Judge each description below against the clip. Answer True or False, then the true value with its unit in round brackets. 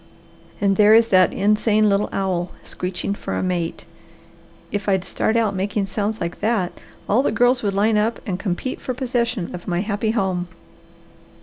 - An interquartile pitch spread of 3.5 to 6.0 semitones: False (3.0 semitones)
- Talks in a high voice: True (205 Hz)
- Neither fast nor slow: True (175 wpm)